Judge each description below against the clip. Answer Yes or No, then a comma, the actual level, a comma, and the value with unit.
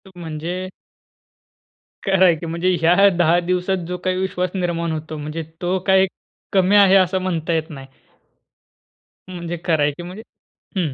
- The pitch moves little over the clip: Yes, narrow, 2.2 semitones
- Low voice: No, medium, 175 Hz